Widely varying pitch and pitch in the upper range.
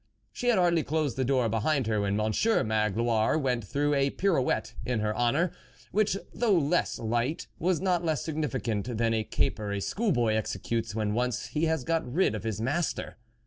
No: wide, 6.6 semitones; low, 125 Hz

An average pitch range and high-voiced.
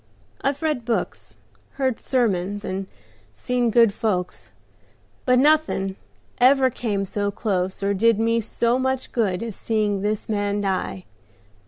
Yes: average, 4.0 semitones; high, 215 Hz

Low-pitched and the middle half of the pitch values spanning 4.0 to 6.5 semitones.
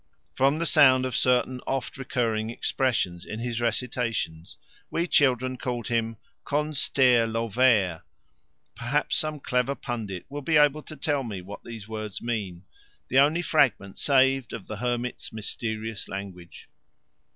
No: low, 120 Hz; average, 3.6 semitones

